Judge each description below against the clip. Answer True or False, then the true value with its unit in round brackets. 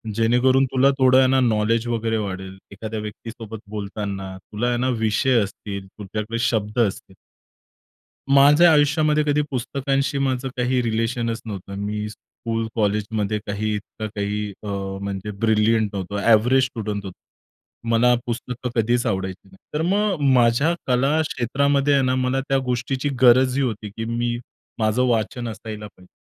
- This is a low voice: True (115 Hz)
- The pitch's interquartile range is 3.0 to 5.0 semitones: True (3.4 semitones)